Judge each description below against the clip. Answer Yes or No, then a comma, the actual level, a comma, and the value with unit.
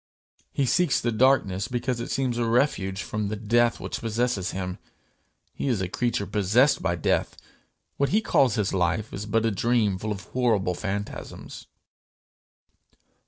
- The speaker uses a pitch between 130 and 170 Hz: No, low, 110 Hz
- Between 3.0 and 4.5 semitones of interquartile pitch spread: Yes, average, 3.8 semitones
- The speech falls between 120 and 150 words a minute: No, average, 160 wpm